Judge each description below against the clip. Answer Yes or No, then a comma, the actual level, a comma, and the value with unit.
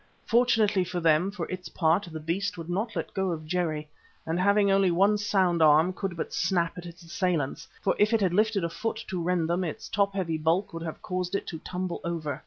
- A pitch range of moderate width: Yes, average, 3.0 semitones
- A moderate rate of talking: No, fast, 225 wpm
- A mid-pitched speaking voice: Yes, medium, 180 Hz